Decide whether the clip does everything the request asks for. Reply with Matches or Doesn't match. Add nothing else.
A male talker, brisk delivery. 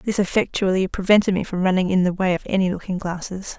Doesn't match